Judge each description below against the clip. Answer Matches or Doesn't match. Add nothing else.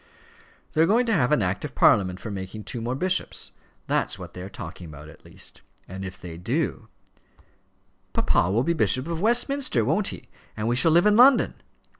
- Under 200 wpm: Doesn't match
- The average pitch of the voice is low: Matches